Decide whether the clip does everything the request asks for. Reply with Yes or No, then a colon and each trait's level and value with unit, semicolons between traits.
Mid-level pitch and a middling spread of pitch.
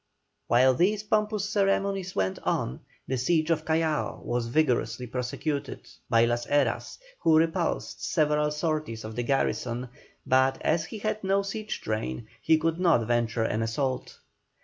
No: medium, 150 Hz; wide, 6.1 semitones